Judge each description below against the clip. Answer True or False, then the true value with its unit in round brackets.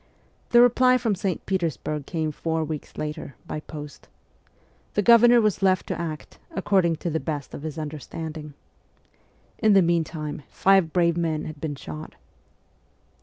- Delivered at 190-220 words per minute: False (155 wpm)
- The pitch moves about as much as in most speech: True (4.0 semitones)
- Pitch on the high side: False (165 Hz)